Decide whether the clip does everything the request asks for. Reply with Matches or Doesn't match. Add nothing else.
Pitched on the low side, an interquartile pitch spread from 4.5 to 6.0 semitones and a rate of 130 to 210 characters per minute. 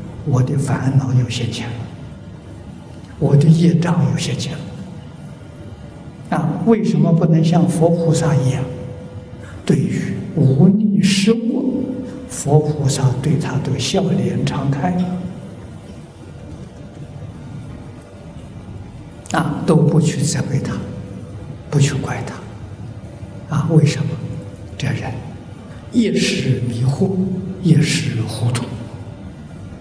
Doesn't match